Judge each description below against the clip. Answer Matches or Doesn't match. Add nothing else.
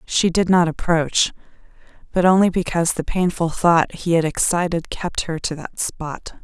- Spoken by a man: Doesn't match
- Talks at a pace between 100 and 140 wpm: Doesn't match